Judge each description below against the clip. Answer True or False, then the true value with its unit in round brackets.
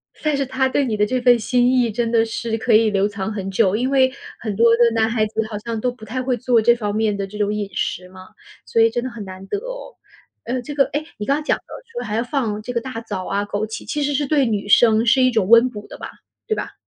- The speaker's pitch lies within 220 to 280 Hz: True (230 Hz)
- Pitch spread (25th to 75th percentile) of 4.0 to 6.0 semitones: False (3.4 semitones)